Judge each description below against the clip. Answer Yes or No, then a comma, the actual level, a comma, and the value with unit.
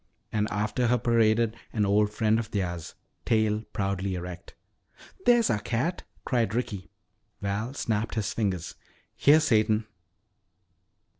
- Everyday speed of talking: No, slow, 125 wpm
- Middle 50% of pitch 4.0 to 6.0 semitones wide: No, narrow, 2.5 semitones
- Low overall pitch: Yes, low, 110 Hz